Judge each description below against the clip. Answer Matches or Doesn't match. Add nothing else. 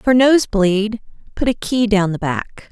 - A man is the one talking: Doesn't match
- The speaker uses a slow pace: Doesn't match